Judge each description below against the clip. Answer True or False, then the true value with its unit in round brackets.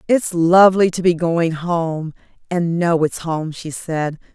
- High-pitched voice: False (170 Hz)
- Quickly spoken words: False (165 wpm)